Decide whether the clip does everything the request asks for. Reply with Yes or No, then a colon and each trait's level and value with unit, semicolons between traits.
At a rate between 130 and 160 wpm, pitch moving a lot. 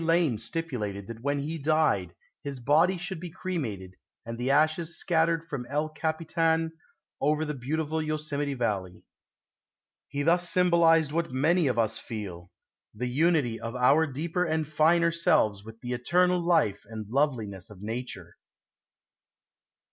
Yes: average, 140 wpm; wide, 5.9 semitones